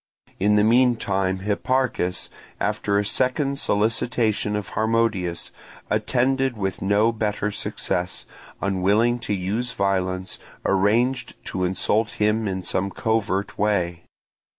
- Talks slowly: Yes, slow, 110 wpm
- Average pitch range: Yes, average, 3.2 semitones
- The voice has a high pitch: No, low, 105 Hz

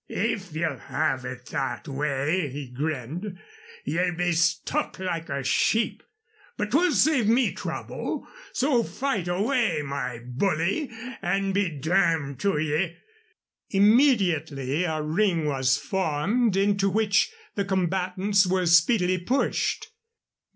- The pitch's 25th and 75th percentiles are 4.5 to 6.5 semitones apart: Yes, average, 5.2 semitones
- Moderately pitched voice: Yes, medium, 180 Hz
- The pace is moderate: No, slow, 120 wpm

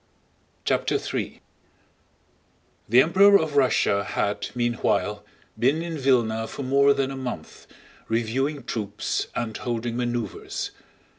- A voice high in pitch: No, low, 125 Hz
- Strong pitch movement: No, average, 3.7 semitones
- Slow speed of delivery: Yes, slow, 115 wpm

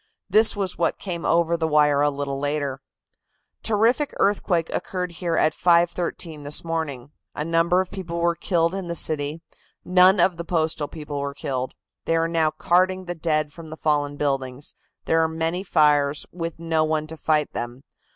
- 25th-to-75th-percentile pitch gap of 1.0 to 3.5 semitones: Yes, average, 2.7 semitones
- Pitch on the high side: No, medium, 165 Hz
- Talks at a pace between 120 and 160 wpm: No, average, 180 wpm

